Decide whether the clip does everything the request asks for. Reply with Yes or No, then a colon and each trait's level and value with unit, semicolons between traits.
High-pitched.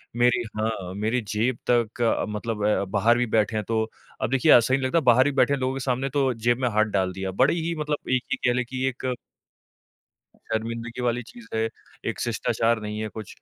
No: low, 120 Hz